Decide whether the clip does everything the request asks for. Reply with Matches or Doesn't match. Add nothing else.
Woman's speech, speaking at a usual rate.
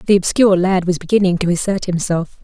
Matches